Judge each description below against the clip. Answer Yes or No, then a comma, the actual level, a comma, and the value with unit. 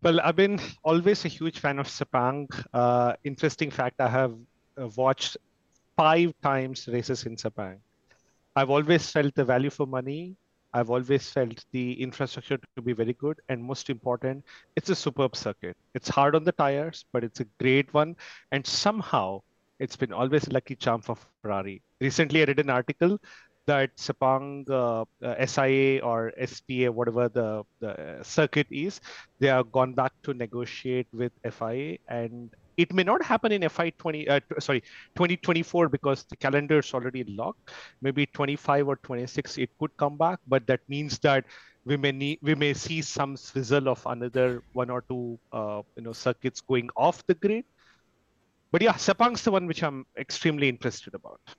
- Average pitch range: Yes, average, 3.4 semitones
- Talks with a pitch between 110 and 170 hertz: Yes, low, 135 Hz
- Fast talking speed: No, average, 175 wpm